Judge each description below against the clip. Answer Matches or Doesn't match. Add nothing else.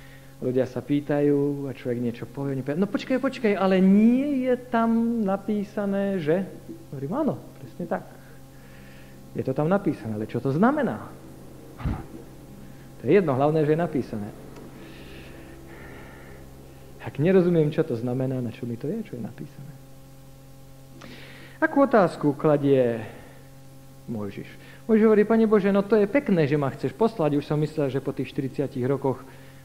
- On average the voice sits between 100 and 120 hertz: Doesn't match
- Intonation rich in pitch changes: Matches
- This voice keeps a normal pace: Matches